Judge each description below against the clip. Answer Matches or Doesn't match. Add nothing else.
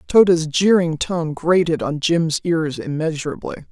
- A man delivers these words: Doesn't match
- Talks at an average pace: Doesn't match